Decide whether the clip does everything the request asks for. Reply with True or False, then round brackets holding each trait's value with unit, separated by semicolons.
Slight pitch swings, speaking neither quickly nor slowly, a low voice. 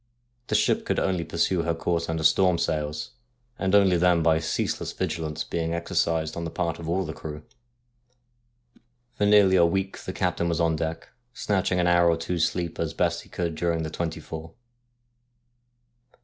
True (1.7 semitones; 175 wpm; 85 Hz)